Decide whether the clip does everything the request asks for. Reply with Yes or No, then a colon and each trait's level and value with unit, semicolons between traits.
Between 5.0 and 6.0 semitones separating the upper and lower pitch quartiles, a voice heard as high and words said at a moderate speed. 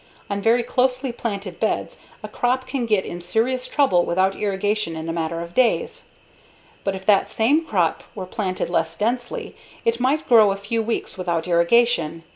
Yes: average, 5.3 semitones; high, 205 Hz; average, 175 wpm